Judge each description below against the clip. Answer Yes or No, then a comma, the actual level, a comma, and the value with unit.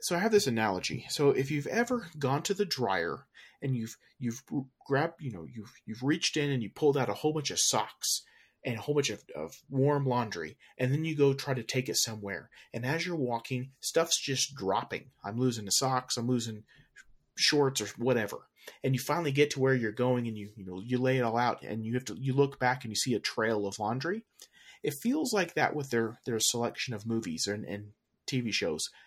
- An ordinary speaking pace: No, fast, 225 wpm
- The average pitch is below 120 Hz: No, low, 130 Hz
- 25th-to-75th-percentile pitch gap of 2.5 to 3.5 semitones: No, average, 4.2 semitones